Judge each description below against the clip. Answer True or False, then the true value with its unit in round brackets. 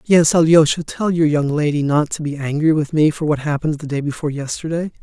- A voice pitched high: False (155 Hz)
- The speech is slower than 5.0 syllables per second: False (6.0 syllables/s)